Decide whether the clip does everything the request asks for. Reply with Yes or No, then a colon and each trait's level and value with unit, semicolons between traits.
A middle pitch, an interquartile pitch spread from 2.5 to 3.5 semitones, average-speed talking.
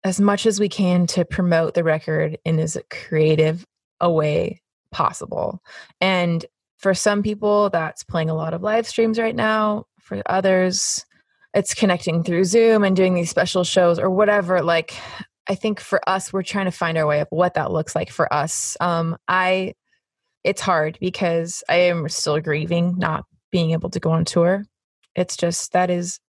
Yes: medium, 180 Hz; average, 2.9 semitones; average, 180 wpm